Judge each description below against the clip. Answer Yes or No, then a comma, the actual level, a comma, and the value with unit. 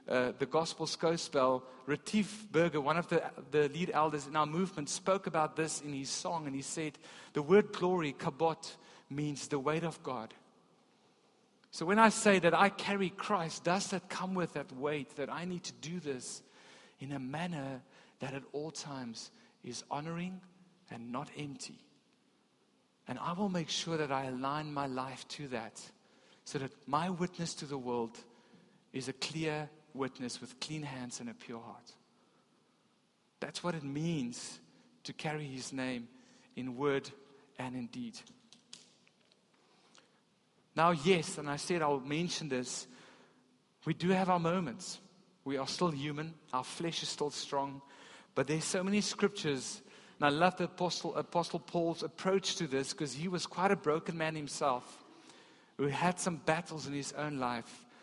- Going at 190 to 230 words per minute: No, average, 170 wpm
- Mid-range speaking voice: Yes, medium, 155 Hz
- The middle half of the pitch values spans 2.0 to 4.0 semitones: No, average, 4.5 semitones